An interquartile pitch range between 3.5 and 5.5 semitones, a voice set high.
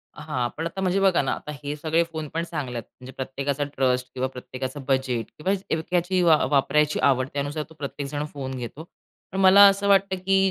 No: average, 4.2 semitones; medium, 150 Hz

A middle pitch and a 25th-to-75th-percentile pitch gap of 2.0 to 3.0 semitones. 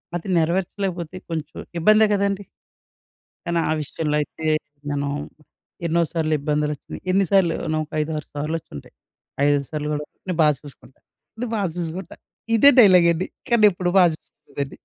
No: medium, 165 Hz; average, 3.8 semitones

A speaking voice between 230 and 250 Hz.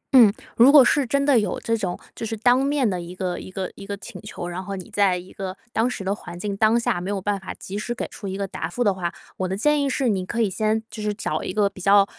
No: high, 205 Hz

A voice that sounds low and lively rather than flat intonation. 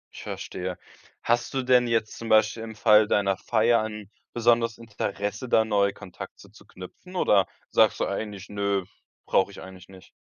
No: low, 105 Hz; narrow, 2.6 semitones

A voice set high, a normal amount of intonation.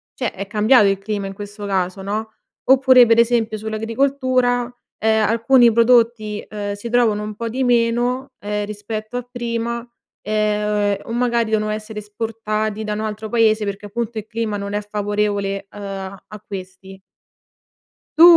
No: high, 215 Hz; narrow, 2.2 semitones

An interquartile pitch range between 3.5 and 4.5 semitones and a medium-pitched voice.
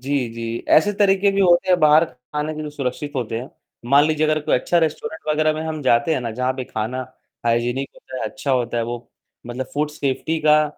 Yes: average, 3.8 semitones; medium, 145 Hz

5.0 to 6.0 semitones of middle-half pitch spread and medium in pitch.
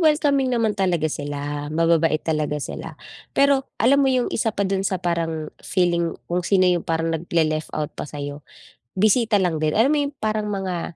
Yes: wide, 5.5 semitones; medium, 175 Hz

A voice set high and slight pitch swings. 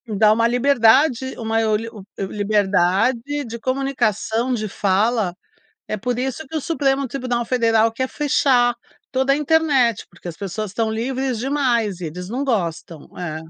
No: high, 235 Hz; average, 3.8 semitones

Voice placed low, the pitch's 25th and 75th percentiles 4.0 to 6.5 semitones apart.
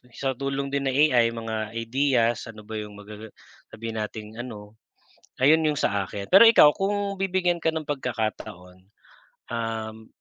Yes: low, 115 Hz; average, 4.6 semitones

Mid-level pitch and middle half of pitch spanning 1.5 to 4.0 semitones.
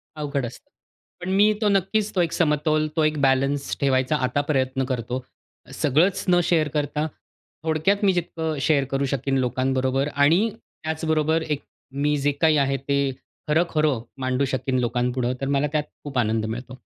Yes: medium, 145 Hz; average, 3.2 semitones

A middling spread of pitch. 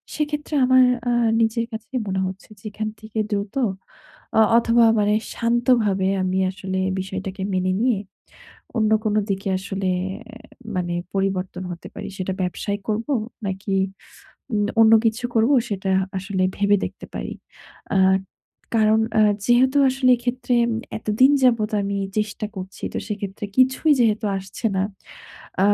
Yes: average, 3.4 semitones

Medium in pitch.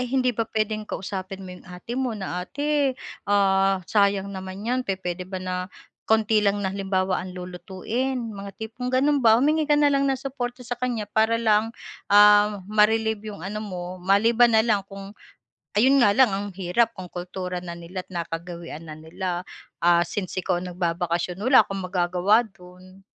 No: high, 200 Hz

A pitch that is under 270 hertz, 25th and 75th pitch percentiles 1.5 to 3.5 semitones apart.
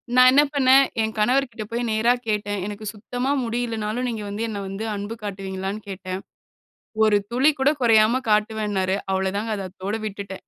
Yes: high, 215 Hz; average, 2.9 semitones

